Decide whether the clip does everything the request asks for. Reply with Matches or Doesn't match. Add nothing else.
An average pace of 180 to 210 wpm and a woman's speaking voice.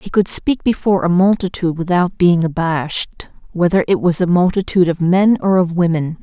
Matches